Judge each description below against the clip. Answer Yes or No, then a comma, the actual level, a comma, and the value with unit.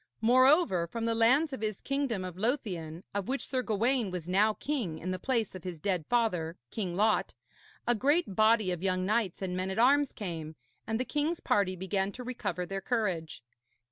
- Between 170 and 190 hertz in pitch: No, high, 210 Hz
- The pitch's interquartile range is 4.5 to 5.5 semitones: Yes, average, 5.0 semitones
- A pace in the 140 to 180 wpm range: No, average, 195 wpm